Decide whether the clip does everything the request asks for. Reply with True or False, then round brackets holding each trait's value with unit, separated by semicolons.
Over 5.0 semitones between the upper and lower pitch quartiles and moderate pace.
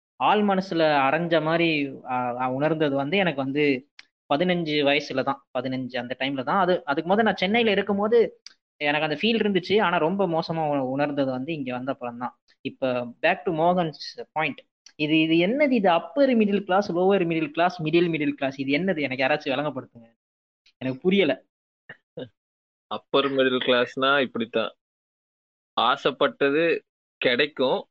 False (5.5 semitones; 135 wpm)